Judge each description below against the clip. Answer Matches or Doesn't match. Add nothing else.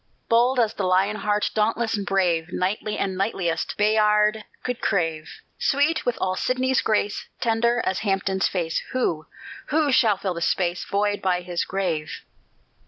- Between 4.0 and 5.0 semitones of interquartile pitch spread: Doesn't match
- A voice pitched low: Doesn't match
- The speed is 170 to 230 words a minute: Doesn't match